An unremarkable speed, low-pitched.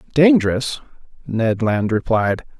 No: slow, 95 wpm; low, 120 Hz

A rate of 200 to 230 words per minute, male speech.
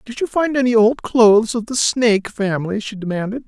Yes: fast, 205 wpm; male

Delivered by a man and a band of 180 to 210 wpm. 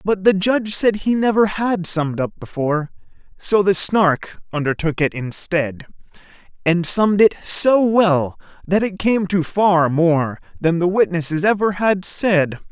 No: male; average, 155 wpm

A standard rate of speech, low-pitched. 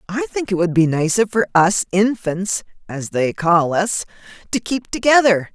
No: average, 175 wpm; high, 195 Hz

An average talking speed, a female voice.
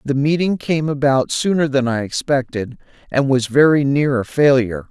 No: average, 170 wpm; male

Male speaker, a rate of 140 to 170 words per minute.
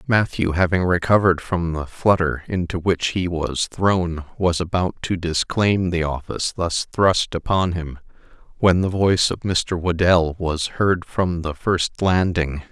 Yes: male; average, 155 wpm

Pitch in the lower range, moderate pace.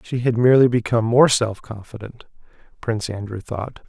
Yes: low, 115 Hz; average, 155 wpm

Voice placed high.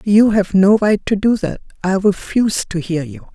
Yes: high, 205 Hz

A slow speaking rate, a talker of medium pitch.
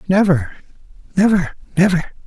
Yes: slow, 80 wpm; medium, 180 Hz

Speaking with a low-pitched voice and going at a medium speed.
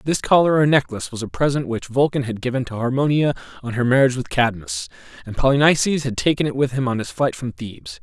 No: low, 130 Hz; fast, 225 wpm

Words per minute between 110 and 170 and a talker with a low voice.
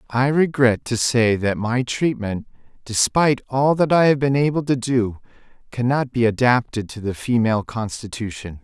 Yes: average, 160 wpm; low, 120 Hz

